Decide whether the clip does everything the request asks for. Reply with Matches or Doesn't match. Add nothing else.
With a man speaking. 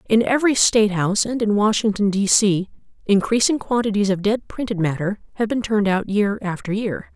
Doesn't match